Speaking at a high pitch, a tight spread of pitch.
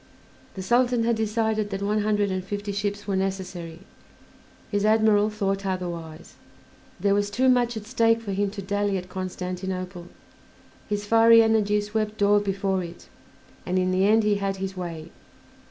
Yes: high, 205 Hz; narrow, 2.2 semitones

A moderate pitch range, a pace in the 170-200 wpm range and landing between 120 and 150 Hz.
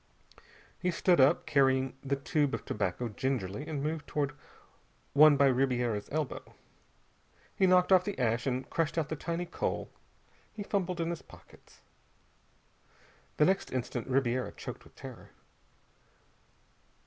No: average, 4.6 semitones; slow, 135 wpm; medium, 140 Hz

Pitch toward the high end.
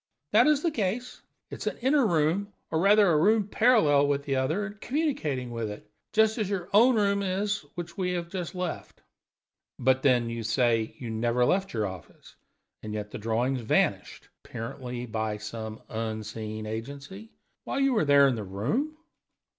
No: medium, 145 Hz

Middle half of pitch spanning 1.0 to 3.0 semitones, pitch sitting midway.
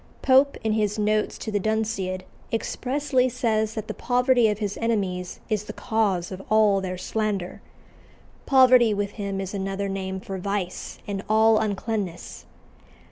No: narrow, 2.5 semitones; high, 210 Hz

